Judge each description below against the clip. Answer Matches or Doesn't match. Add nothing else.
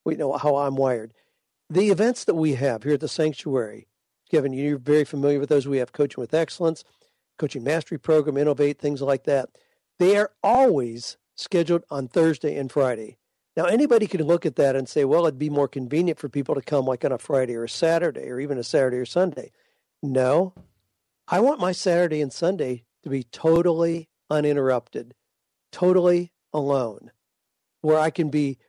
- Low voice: Doesn't match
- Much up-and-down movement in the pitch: Doesn't match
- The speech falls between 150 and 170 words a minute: Doesn't match